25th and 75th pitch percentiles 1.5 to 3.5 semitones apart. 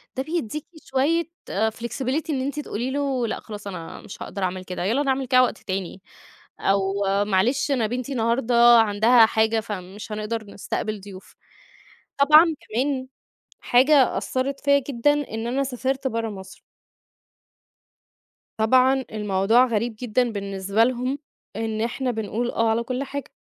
No: average, 3.9 semitones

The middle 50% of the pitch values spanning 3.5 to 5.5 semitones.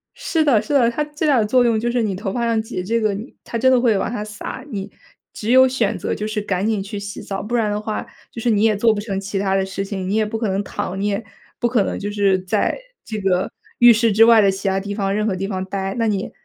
No: average, 2.9 semitones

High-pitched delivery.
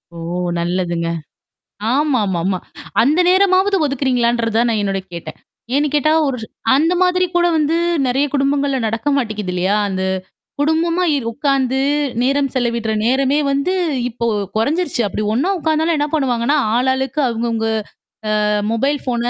Yes: very high, 265 Hz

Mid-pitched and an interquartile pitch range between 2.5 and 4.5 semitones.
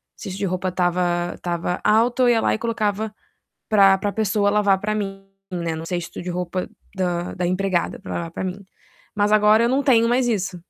No: high, 195 Hz; average, 3.1 semitones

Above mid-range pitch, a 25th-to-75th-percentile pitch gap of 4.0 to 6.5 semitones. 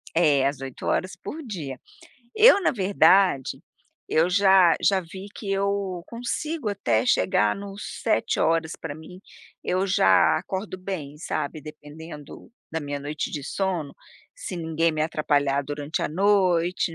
No: medium, 165 Hz; average, 4.7 semitones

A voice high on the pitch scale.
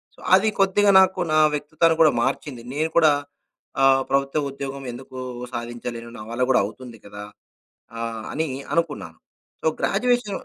No: medium, 140 Hz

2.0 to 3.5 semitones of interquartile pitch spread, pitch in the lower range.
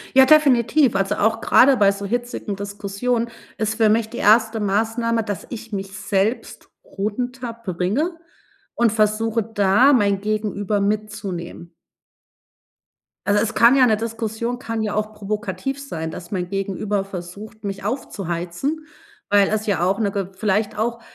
No: average, 2.7 semitones; high, 215 Hz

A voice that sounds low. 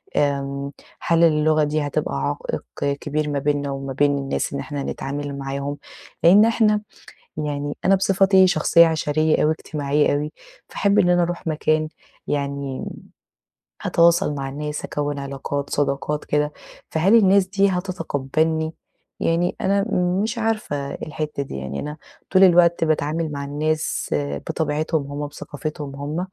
No: medium, 150 Hz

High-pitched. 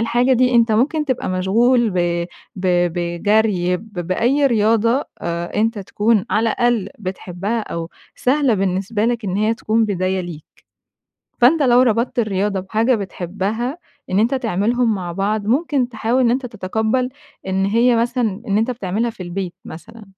Yes: high, 220 Hz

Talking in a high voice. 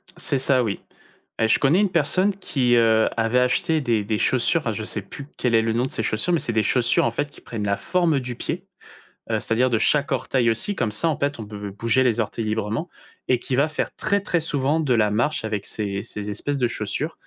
No: low, 120 Hz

